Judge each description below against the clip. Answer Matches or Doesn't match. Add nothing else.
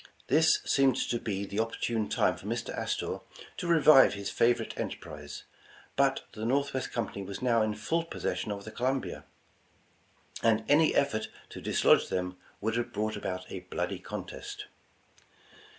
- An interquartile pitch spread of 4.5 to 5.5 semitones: Matches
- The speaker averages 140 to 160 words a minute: Matches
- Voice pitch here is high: Doesn't match